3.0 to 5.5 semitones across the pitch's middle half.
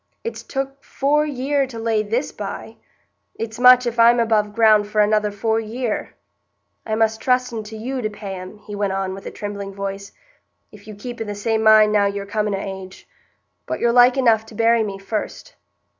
No: narrow, 2.6 semitones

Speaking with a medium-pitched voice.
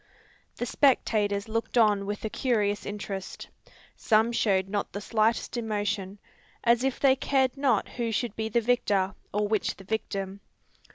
No: high, 215 Hz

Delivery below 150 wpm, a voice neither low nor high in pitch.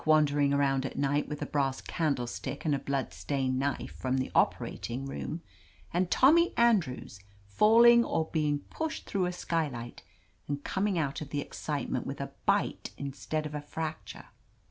No: average, 165 wpm; medium, 145 Hz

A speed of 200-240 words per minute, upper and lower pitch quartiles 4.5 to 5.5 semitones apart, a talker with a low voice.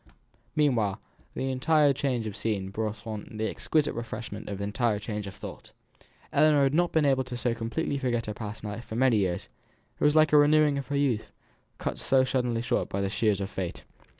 Yes: fast, 205 wpm; average, 4.9 semitones; low, 120 Hz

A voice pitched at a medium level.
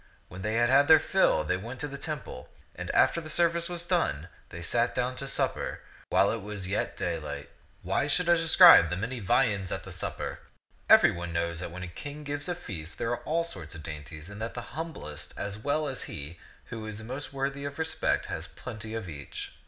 No: low, 115 Hz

